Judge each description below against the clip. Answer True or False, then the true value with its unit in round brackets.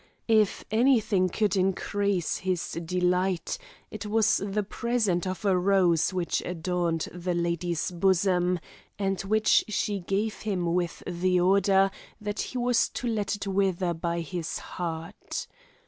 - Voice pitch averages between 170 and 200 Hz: True (185 Hz)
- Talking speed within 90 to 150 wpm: True (140 wpm)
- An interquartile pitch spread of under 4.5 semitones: True (2.6 semitones)